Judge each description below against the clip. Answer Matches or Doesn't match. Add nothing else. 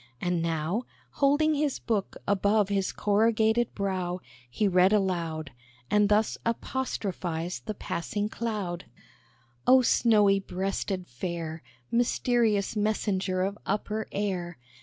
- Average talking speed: Doesn't match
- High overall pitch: Matches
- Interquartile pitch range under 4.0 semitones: Matches